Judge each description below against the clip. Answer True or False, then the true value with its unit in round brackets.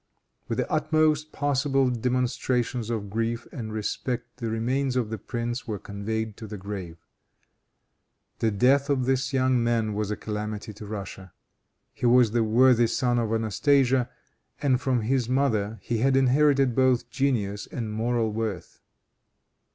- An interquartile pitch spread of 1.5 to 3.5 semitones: True (3.2 semitones)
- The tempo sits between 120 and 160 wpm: True (150 wpm)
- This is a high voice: False (120 Hz)